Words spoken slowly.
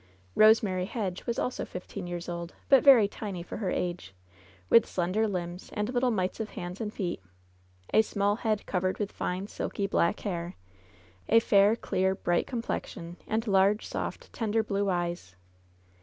No: average, 160 wpm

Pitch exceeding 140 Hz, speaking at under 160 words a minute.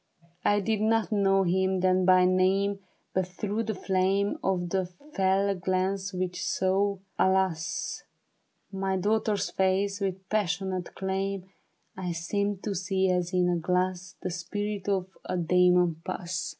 Yes: high, 190 Hz; average, 140 wpm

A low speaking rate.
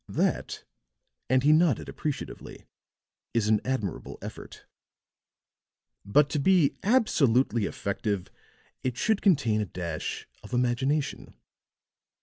Yes: slow, 105 wpm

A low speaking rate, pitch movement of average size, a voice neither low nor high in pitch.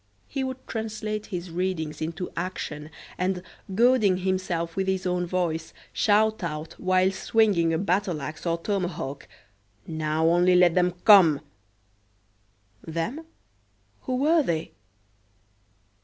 Yes: slow, 120 wpm; average, 3.7 semitones; medium, 180 Hz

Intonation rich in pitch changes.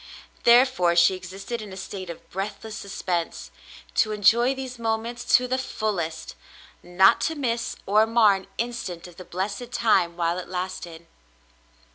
No: average, 4.7 semitones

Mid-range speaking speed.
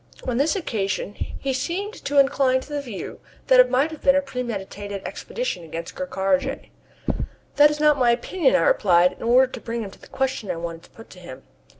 No: fast, 220 wpm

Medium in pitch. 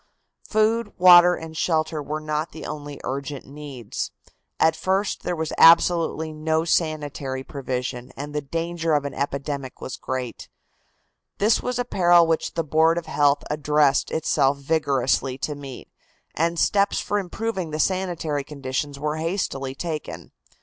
Yes: medium, 155 Hz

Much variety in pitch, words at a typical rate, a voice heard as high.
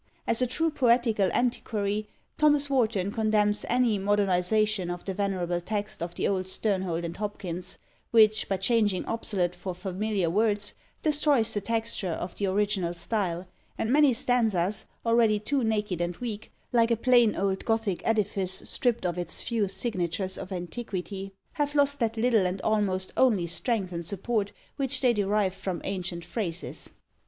No: average, 3.7 semitones; average, 155 wpm; high, 205 Hz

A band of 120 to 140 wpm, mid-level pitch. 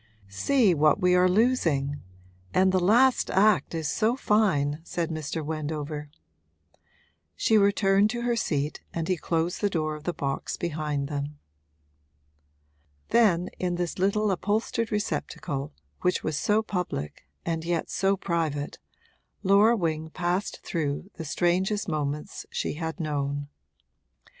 Yes: slow, 135 wpm; medium, 170 Hz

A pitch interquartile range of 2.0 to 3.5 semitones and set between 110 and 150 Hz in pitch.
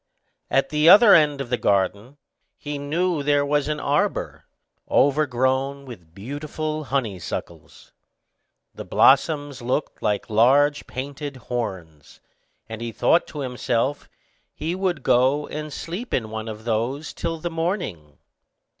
No: average, 4.4 semitones; medium, 140 Hz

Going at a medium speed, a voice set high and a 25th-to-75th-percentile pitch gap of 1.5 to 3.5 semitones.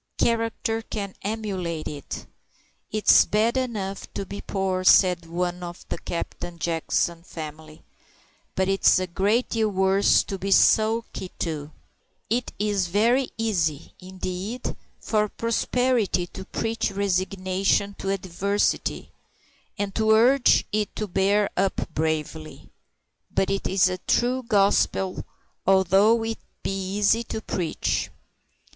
No: slow, 125 wpm; high, 195 Hz; average, 3.2 semitones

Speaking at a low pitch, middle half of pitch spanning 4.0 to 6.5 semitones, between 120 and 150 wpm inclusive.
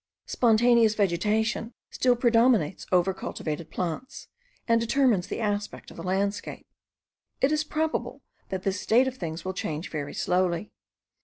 No: high, 210 Hz; average, 4.8 semitones; average, 140 wpm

